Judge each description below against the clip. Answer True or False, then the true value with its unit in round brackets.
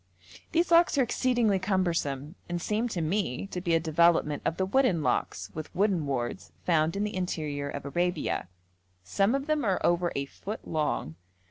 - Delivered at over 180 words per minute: False (175 wpm)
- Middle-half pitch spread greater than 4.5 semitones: True (5.3 semitones)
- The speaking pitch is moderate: True (175 Hz)